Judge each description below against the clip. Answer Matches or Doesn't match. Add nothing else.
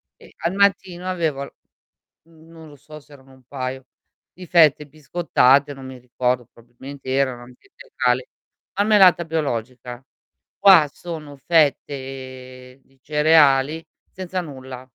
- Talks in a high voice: Doesn't match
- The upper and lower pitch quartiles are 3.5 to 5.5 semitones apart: Matches